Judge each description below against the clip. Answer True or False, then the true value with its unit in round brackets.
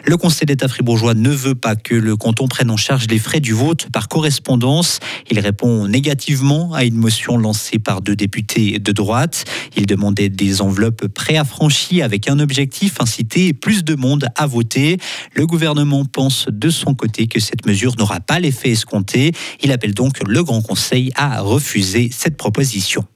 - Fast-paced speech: False (175 wpm)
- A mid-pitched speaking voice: False (125 Hz)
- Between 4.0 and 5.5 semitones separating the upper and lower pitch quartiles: True (4.5 semitones)